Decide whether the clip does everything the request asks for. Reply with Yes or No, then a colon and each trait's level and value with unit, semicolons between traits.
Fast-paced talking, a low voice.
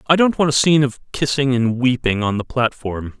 Yes: fast, 225 wpm; low, 130 Hz